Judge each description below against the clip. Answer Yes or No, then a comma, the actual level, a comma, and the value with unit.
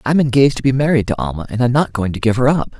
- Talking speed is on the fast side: Yes, fast, 320 wpm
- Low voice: Yes, low, 125 Hz